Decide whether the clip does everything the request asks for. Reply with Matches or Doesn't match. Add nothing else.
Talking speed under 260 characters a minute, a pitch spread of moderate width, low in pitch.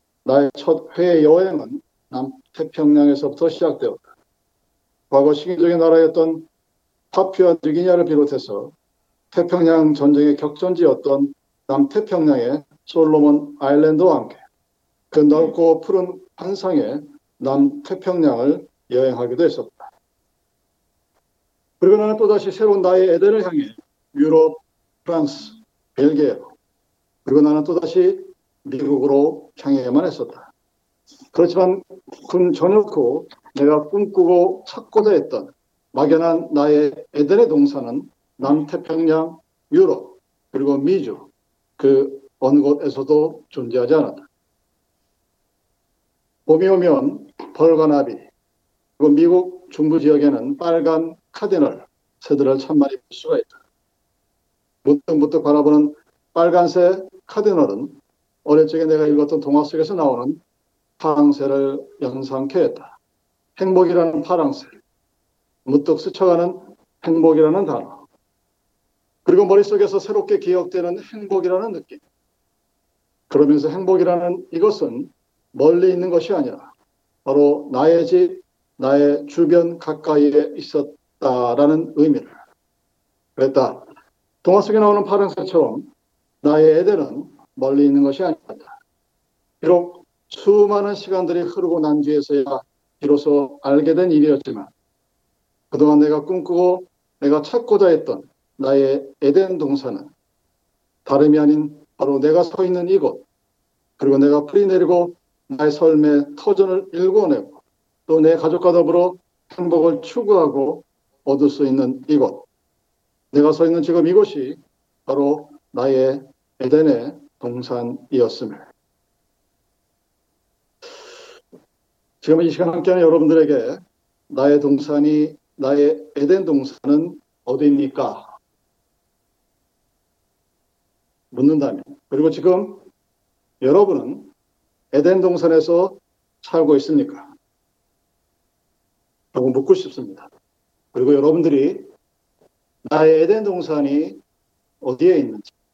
Doesn't match